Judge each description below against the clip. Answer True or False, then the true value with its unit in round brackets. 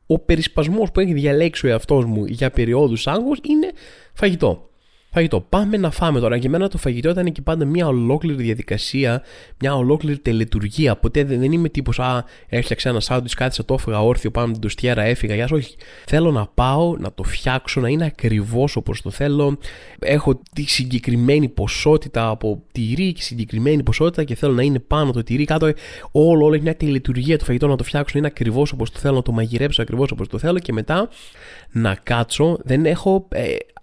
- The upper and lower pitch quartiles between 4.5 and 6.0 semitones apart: True (4.8 semitones)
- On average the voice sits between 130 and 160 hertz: True (135 Hz)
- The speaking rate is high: True (190 wpm)